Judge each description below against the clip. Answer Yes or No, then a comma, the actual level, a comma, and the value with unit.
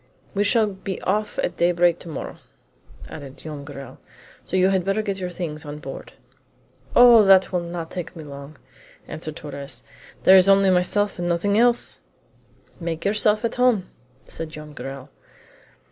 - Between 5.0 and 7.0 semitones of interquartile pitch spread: No, average, 4.5 semitones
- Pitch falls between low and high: Yes, medium, 180 Hz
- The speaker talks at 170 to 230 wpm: No, average, 160 wpm